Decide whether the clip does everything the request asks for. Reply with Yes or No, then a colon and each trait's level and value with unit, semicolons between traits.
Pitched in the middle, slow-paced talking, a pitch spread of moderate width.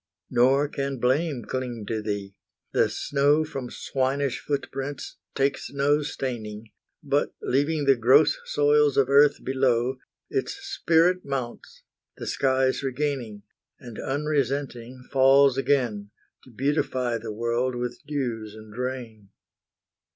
No: low, 130 Hz; slow, 120 wpm; average, 3.0 semitones